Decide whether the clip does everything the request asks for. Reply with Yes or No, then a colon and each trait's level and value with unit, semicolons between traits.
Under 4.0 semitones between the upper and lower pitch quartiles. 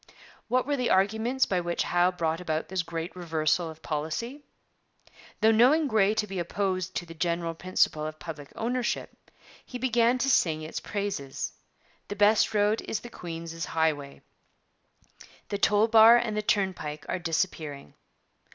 No: average, 5.2 semitones